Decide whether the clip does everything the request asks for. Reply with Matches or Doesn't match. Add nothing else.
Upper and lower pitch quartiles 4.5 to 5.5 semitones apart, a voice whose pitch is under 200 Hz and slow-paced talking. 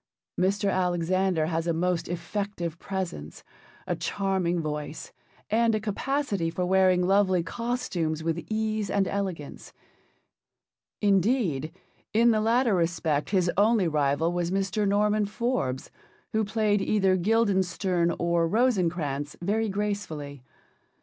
Doesn't match